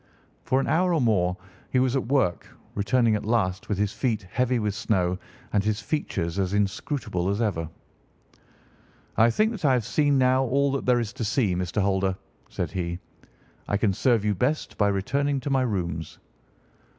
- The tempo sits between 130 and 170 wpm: No, average, 185 wpm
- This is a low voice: Yes, low, 110 Hz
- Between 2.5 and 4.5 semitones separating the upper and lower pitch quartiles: No, average, 5.2 semitones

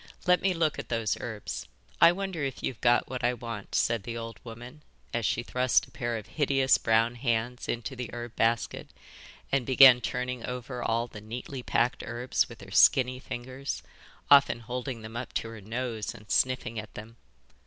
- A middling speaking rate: Yes, average, 185 wpm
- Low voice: Yes, low, 120 Hz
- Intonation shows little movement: Yes, narrow, 2.0 semitones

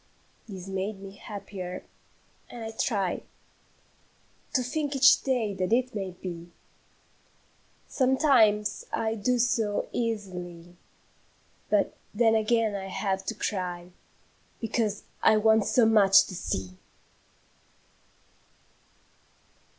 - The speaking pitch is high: Yes, high, 210 Hz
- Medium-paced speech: No, slow, 105 wpm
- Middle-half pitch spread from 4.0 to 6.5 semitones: No, average, 3.2 semitones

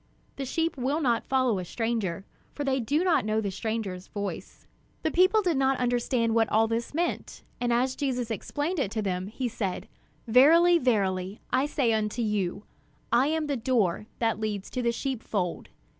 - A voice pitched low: No, high, 235 Hz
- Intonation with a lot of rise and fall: No, average, 4.2 semitones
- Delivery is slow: No, average, 180 wpm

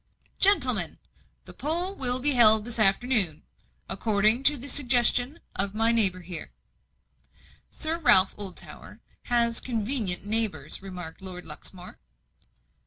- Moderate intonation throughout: Yes, average, 4.7 semitones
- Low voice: No, high, 225 Hz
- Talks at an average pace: No, slow, 115 wpm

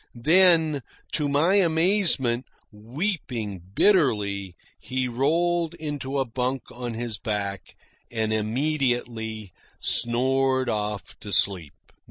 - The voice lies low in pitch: Yes, low, 125 Hz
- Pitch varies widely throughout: Yes, wide, 5.9 semitones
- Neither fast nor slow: No, slow, 100 wpm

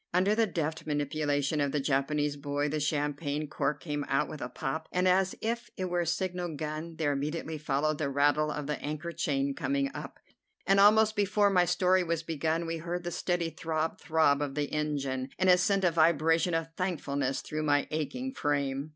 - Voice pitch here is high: No, medium, 155 Hz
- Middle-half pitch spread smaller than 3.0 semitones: No, average, 3.4 semitones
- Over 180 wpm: Yes, average, 195 wpm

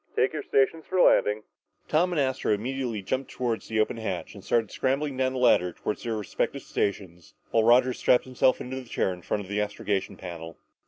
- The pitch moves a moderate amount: Yes, average, 4.2 semitones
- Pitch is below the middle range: Yes, low, 115 Hz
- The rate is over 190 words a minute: Yes, fast, 205 wpm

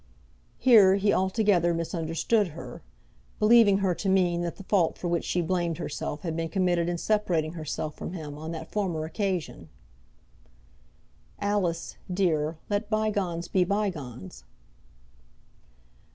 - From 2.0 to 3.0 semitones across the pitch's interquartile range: No, average, 3.4 semitones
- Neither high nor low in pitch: Yes, medium, 175 Hz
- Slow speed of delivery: Yes, slow, 130 wpm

